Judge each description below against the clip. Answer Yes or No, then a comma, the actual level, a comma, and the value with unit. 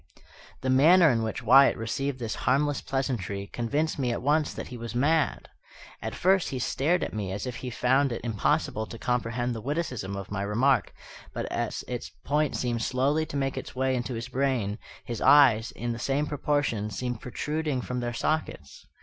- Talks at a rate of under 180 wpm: No, average, 190 wpm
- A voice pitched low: Yes, low, 125 Hz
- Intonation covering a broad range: No, average, 3.6 semitones